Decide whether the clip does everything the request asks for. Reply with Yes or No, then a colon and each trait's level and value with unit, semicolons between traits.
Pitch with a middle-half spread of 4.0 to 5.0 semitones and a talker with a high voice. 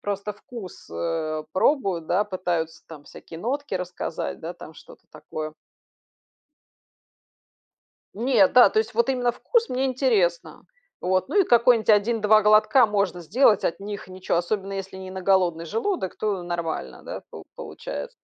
Yes: average, 4.7 semitones; high, 195 Hz